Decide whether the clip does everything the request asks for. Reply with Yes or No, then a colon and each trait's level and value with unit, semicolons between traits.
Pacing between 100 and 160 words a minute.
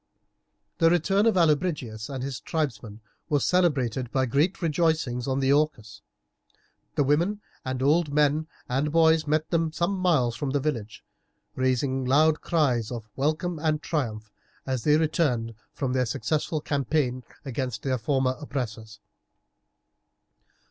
Yes: slow, 135 wpm